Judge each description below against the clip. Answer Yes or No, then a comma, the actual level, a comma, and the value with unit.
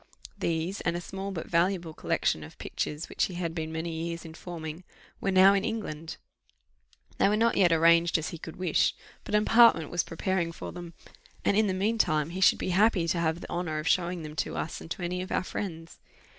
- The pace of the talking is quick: Yes, fast, 225 wpm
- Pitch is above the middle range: No, medium, 170 Hz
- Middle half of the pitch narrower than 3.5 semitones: Yes, narrow, 2.6 semitones